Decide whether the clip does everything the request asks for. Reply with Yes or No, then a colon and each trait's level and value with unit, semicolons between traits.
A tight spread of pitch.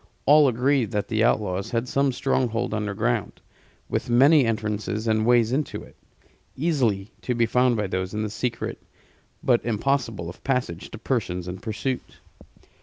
No: average, 3.3 semitones